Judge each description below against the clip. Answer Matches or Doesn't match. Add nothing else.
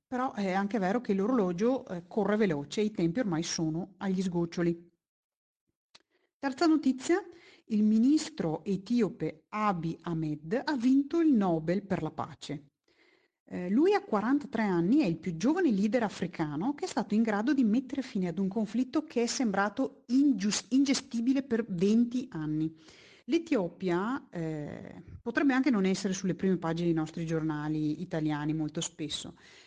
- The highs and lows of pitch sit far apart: Matches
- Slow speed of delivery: Doesn't match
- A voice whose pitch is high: Matches